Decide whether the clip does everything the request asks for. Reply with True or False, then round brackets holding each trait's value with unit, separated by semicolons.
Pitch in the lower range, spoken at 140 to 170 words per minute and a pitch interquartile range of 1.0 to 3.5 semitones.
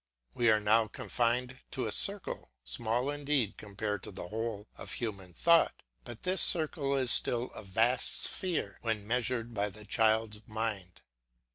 True (115 Hz; 155 wpm; 3.2 semitones)